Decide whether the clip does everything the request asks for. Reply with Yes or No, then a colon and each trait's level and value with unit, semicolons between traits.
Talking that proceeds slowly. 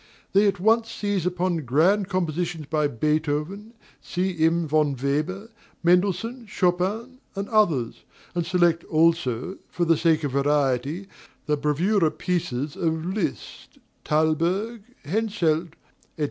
Yes: slow, 120 wpm